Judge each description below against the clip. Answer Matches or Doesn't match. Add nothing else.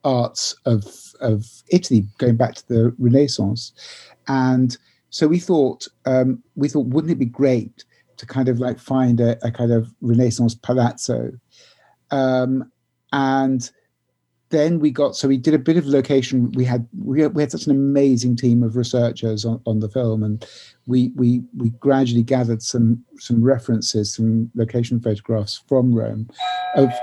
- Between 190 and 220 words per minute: Doesn't match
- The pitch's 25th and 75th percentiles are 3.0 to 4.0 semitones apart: Doesn't match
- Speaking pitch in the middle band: Doesn't match